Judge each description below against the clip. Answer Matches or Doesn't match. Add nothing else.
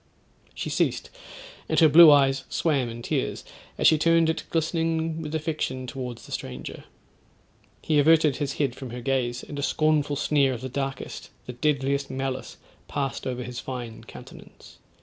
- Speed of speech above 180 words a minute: Doesn't match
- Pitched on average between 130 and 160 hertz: Matches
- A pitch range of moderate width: Matches